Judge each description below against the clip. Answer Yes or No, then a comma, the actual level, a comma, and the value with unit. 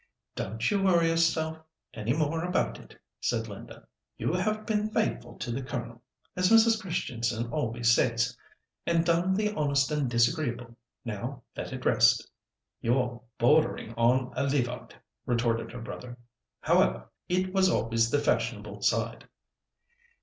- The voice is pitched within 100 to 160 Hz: Yes, medium, 140 Hz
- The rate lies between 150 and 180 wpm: No, slow, 135 wpm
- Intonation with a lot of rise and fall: Yes, wide, 6.5 semitones